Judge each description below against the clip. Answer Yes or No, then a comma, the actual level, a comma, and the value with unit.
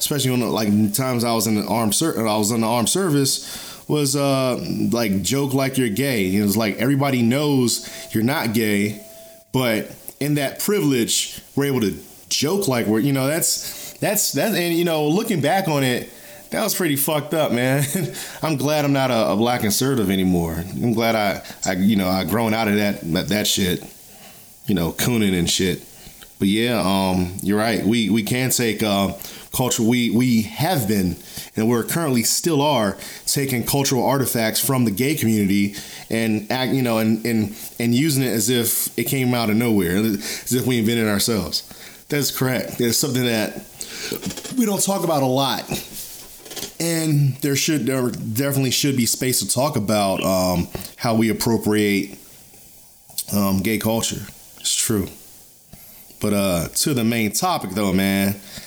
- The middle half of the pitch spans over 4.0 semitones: Yes, average, 4.4 semitones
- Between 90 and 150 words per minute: No, average, 180 wpm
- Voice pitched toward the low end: Yes, low, 120 Hz